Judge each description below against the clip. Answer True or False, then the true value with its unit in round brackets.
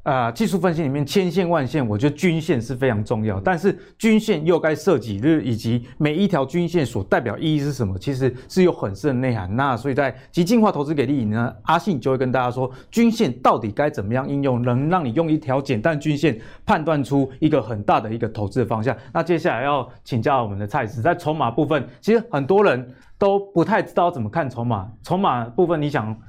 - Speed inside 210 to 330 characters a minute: False (340 characters per minute)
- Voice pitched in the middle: True (145 Hz)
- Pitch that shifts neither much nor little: False (5.7 semitones)